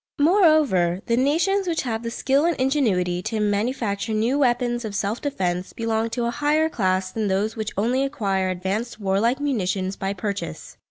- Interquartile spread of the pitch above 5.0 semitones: Yes, wide, 5.6 semitones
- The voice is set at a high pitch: Yes, high, 225 Hz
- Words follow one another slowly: No, average, 170 wpm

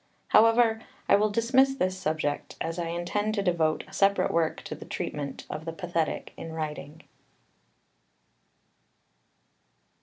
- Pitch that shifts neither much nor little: Yes, average, 5.0 semitones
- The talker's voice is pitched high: No, medium, 175 Hz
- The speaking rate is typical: No, slow, 130 wpm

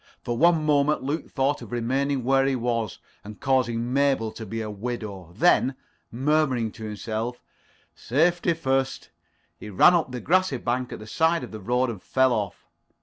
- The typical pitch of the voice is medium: No, low, 125 Hz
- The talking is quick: No, average, 175 wpm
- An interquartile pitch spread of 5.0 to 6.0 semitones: No, average, 3.8 semitones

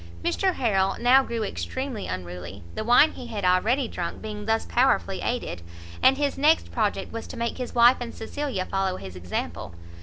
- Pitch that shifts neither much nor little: Yes, average, 5.0 semitones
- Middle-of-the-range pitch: No, high, 225 Hz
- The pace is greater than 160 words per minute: Yes, average, 180 wpm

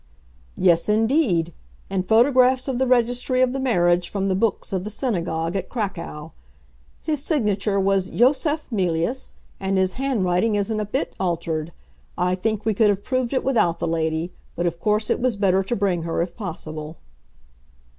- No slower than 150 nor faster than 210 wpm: Yes, average, 170 wpm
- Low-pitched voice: No, high, 195 Hz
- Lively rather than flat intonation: Yes, wide, 5.7 semitones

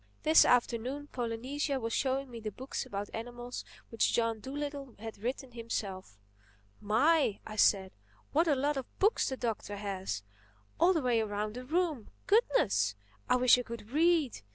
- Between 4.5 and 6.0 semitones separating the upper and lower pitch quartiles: Yes, average, 5.0 semitones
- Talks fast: No, average, 155 wpm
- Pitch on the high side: Yes, high, 240 Hz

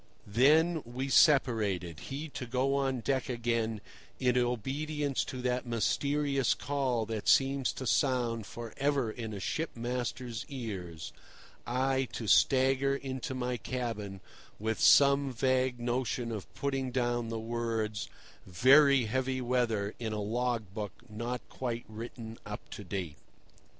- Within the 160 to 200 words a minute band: No, slow, 135 wpm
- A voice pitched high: No, low, 125 Hz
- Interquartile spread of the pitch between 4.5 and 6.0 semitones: No, average, 3.0 semitones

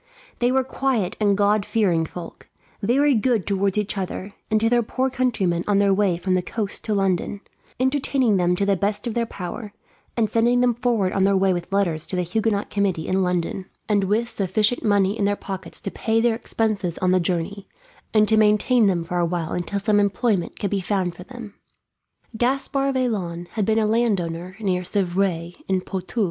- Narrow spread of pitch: No, average, 3.4 semitones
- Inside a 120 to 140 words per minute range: No, average, 200 wpm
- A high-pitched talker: Yes, high, 200 Hz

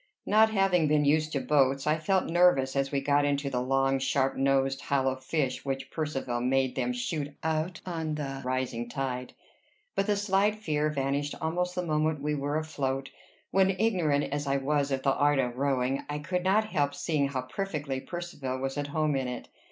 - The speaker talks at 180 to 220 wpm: Yes, average, 190 wpm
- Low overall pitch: No, medium, 145 Hz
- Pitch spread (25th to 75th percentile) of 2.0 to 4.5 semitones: Yes, average, 2.9 semitones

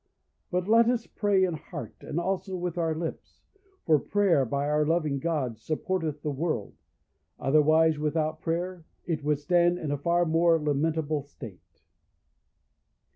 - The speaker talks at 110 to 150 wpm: Yes, average, 145 wpm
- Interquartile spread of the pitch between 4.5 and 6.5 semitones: No, average, 2.9 semitones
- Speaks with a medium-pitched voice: Yes, medium, 160 Hz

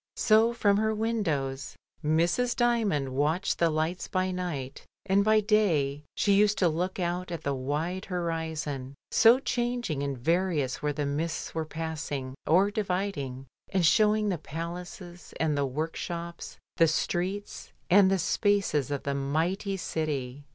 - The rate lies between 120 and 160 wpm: Yes, average, 150 wpm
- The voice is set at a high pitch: No, medium, 170 Hz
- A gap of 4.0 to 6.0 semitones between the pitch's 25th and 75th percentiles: Yes, average, 5.2 semitones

